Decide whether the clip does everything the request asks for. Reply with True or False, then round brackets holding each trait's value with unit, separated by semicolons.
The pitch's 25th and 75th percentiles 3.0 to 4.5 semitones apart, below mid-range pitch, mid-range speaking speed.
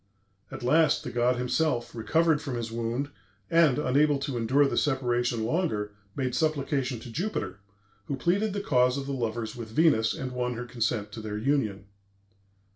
True (4.0 semitones; 125 Hz; 170 wpm)